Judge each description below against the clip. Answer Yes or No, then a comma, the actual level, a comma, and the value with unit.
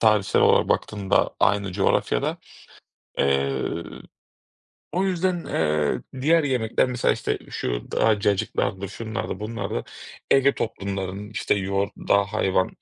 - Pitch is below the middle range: Yes, low, 100 Hz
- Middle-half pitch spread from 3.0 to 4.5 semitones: Yes, average, 3.3 semitones